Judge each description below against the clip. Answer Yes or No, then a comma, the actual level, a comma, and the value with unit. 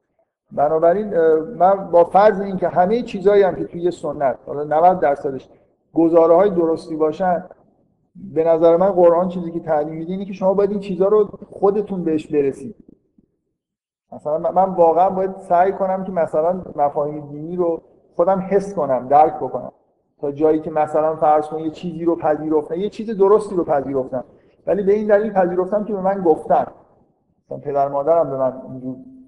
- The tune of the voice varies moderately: Yes, average, 3.8 semitones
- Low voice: No, medium, 170 Hz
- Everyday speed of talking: No, fast, 165 wpm